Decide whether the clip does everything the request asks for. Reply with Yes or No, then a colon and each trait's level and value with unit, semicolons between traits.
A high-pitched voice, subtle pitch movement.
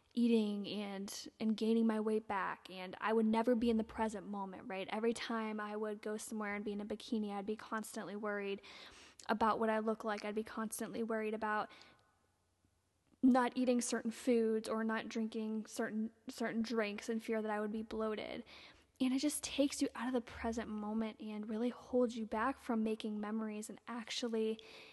Yes: high, 220 Hz; narrow, 1.5 semitones